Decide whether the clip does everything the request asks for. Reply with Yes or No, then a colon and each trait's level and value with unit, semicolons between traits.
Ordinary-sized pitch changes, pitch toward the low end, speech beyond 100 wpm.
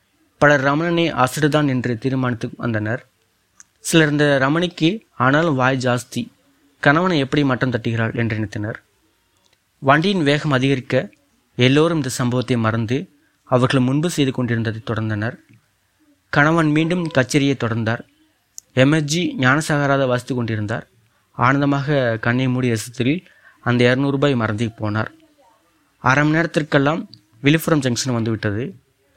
Yes: average, 3.9 semitones; low, 130 Hz; average, 110 wpm